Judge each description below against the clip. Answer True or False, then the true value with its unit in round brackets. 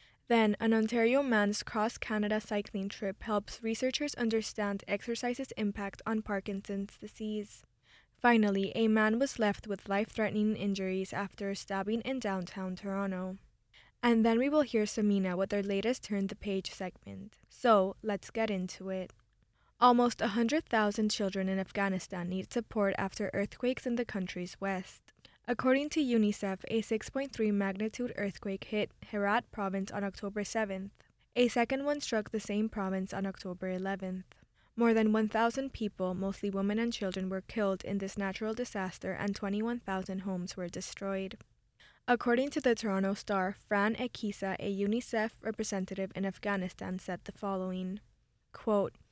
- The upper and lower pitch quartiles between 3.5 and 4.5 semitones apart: False (2.6 semitones)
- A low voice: False (205 Hz)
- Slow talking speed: False (145 wpm)